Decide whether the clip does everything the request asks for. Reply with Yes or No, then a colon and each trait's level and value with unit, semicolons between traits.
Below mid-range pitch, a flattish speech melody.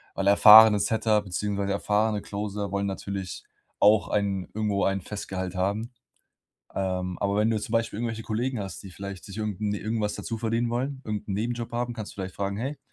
Yes: low, 105 Hz; narrow, 2.1 semitones